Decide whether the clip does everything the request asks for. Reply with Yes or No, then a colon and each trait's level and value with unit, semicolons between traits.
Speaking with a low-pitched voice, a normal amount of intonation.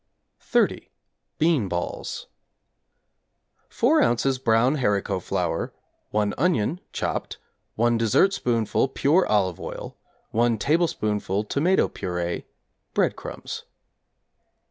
No: low, 115 Hz; wide, 6.6 semitones